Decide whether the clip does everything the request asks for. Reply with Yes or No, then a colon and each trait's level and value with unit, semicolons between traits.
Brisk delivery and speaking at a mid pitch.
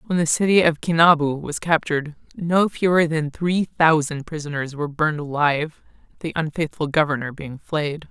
No: average, 155 wpm; medium, 155 Hz